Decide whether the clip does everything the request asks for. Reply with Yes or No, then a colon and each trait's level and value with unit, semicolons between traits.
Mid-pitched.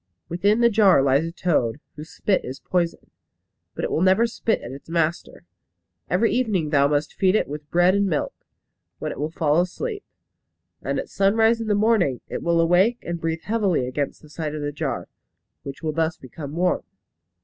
Yes: medium, 170 Hz